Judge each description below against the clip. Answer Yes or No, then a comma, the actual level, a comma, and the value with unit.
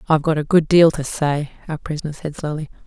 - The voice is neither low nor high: Yes, medium, 155 Hz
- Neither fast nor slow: No, fast, 230 wpm